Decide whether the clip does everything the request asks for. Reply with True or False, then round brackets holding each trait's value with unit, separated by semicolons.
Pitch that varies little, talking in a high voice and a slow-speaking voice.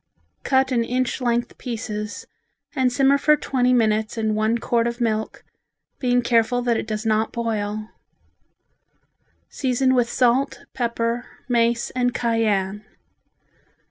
True (2.2 semitones; 235 Hz; 125 wpm)